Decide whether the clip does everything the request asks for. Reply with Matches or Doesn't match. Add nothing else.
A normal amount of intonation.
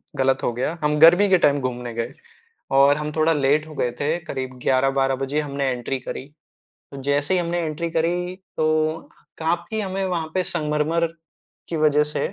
Matches